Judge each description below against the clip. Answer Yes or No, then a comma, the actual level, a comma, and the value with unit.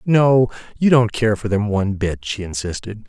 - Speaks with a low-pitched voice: Yes, low, 110 Hz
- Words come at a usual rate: Yes, average, 195 wpm